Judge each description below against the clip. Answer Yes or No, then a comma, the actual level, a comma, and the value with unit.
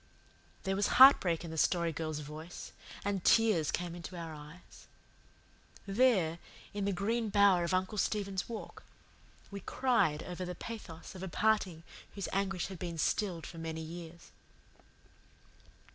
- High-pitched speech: No, medium, 180 Hz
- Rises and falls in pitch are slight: No, average, 3.4 semitones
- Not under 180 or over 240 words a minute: No, average, 145 wpm